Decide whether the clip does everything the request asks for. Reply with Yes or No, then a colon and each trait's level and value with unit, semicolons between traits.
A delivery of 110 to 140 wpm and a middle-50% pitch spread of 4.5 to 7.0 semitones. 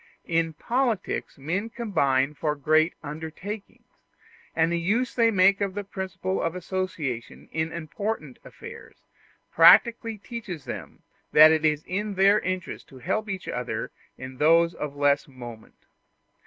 Yes: slow, 135 wpm; average, 4.9 semitones